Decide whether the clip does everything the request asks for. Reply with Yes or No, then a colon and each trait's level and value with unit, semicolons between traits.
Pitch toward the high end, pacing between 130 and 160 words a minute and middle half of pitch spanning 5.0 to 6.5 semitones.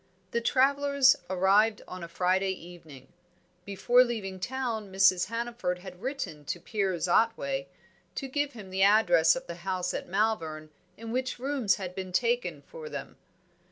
Yes: high, 195 Hz; average, 155 wpm; average, 5.3 semitones